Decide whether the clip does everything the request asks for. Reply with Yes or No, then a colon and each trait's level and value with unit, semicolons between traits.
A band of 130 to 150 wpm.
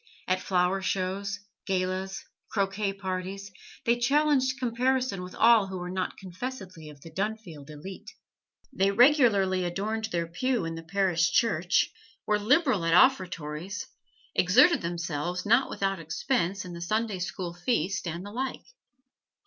Yes: average, 140 wpm